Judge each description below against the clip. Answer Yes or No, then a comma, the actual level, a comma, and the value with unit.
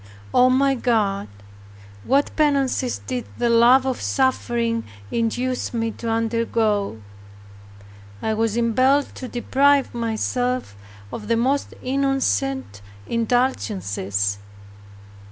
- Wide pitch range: No, average, 2.7 semitones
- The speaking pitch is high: Yes, high, 240 Hz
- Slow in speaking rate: Yes, slow, 100 wpm